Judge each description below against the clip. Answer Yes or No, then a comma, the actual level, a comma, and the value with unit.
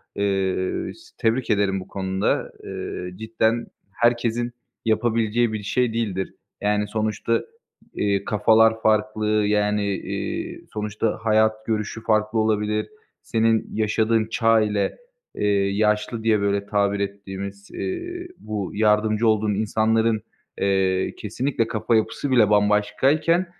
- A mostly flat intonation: Yes, narrow, 1.7 semitones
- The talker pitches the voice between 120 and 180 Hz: No, low, 110 Hz